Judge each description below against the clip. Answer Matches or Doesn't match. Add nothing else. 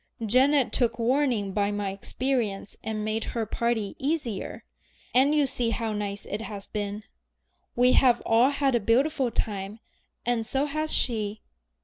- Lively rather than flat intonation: Doesn't match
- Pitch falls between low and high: Doesn't match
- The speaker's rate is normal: Matches